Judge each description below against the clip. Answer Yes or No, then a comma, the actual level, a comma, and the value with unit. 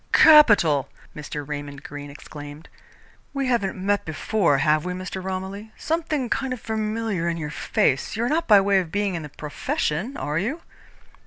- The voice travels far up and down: Yes, wide, 6.7 semitones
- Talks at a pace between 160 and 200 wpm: Yes, average, 170 wpm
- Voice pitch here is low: No, high, 190 Hz